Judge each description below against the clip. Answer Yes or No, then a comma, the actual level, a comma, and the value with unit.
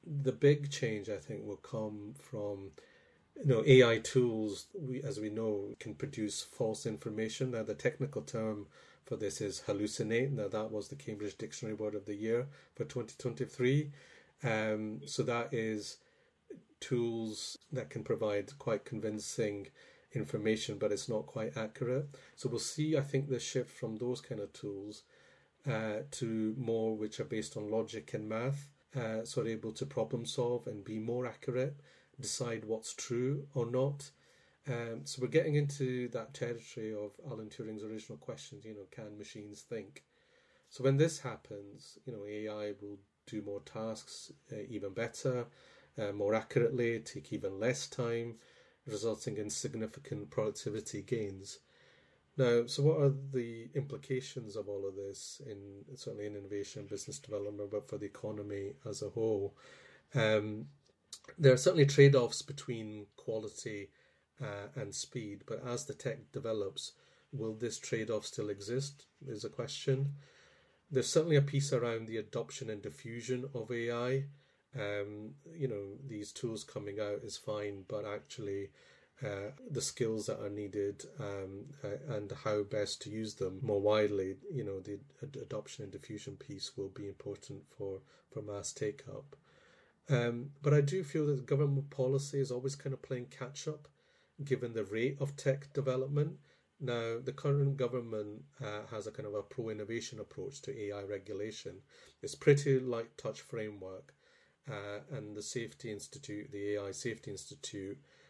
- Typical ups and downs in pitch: Yes, average, 4.3 semitones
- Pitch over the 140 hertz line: No, low, 115 Hz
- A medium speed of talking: Yes, average, 160 wpm